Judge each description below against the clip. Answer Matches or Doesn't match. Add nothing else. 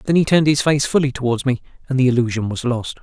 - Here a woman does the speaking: Doesn't match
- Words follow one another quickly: Matches